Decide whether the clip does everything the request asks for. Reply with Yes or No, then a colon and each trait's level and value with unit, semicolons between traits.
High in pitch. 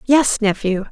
Yes: high, 220 Hz